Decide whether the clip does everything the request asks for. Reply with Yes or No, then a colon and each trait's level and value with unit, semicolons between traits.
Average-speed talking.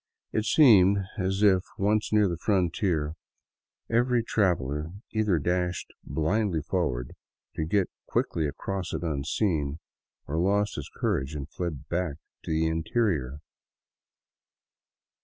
No: slow, 120 wpm